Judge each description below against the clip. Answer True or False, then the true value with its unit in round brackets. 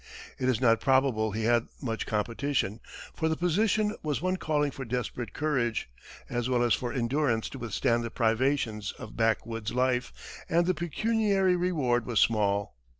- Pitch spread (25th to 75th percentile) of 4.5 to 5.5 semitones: True (5.2 semitones)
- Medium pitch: False (125 Hz)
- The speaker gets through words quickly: False (165 wpm)